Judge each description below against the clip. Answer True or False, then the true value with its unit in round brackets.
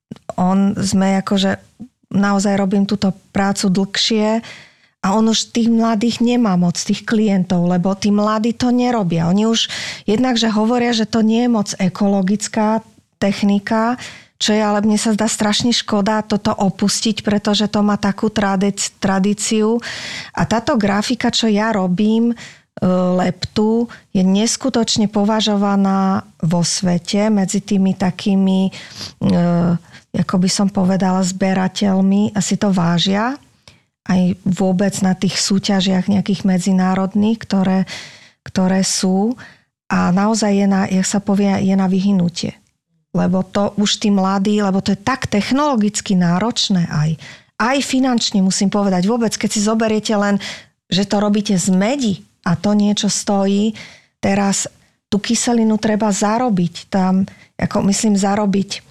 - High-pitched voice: True (200 Hz)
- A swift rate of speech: False (140 wpm)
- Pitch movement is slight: True (2.3 semitones)